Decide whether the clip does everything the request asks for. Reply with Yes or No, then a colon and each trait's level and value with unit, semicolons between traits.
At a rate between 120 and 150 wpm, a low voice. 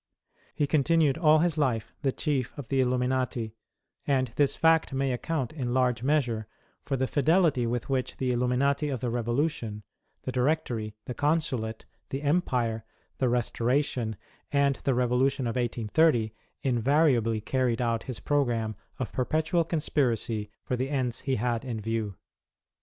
Yes: average, 145 wpm; low, 130 Hz